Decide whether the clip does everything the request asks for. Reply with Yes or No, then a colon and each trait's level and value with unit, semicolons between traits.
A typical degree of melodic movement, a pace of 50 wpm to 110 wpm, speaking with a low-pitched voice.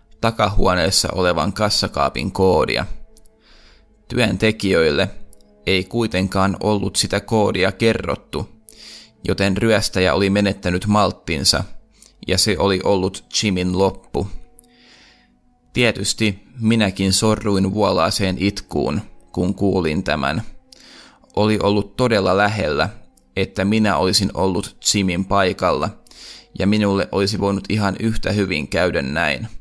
No: narrow, 2.3 semitones; average, 100 wpm; low, 100 Hz